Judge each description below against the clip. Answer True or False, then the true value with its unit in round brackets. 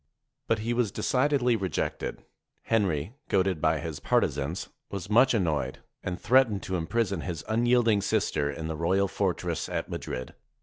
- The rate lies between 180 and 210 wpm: False (160 wpm)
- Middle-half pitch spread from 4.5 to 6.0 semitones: True (5.6 semitones)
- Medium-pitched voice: False (95 Hz)